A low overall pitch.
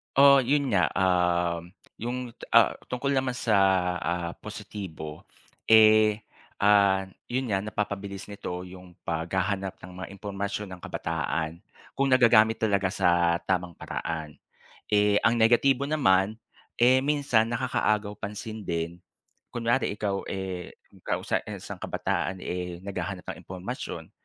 Yes: low, 100 Hz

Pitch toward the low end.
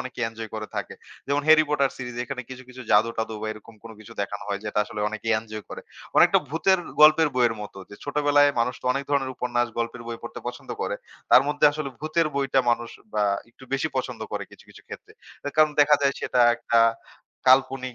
Yes: low, 125 Hz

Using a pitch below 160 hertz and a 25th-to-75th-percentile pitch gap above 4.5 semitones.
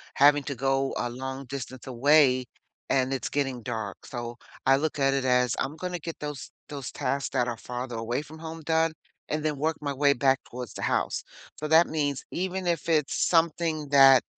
No: medium, 140 Hz; average, 3.2 semitones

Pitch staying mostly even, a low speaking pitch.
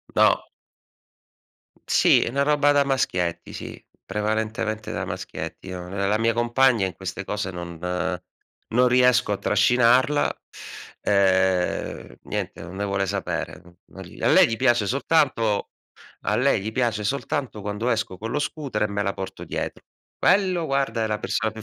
No: average, 4.5 semitones; low, 110 Hz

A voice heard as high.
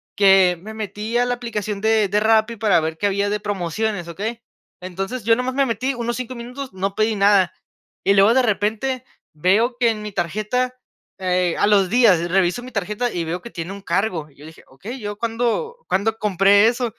Yes: high, 210 Hz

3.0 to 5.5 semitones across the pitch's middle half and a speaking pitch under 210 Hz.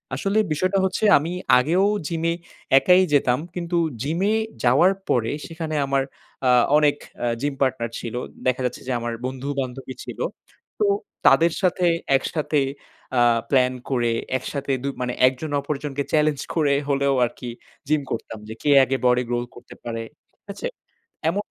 Yes: average, 4.4 semitones; medium, 140 Hz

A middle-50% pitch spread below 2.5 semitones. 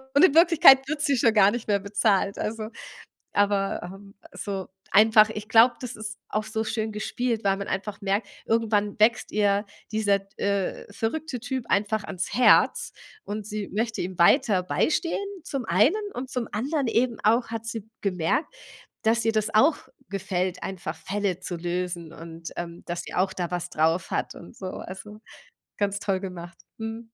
No: average, 2.9 semitones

